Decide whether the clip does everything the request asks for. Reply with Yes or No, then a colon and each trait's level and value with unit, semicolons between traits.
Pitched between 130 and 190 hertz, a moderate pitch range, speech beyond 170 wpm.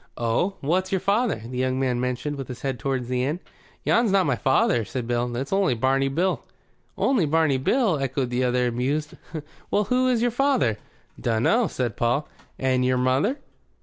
No: low, 135 Hz; wide, 7.0 semitones; average, 180 wpm